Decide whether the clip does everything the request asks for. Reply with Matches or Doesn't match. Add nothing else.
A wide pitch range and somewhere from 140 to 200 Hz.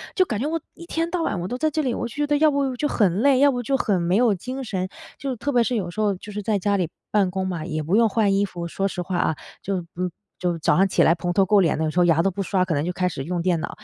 Matches